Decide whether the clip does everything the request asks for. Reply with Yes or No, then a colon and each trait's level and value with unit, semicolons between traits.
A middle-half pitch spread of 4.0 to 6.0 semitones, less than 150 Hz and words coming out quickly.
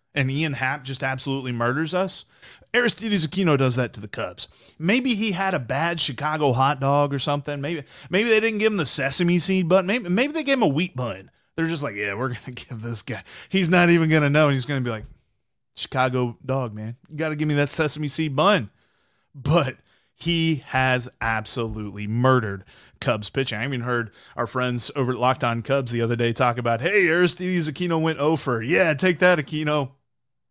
Yes: average, 5.3 semitones; medium, 140 Hz; fast, 210 wpm